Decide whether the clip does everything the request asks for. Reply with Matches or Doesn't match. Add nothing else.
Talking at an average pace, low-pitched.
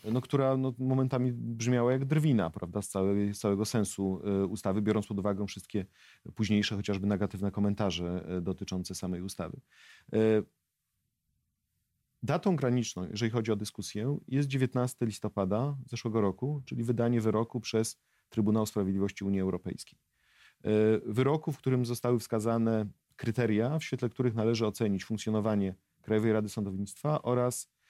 Matches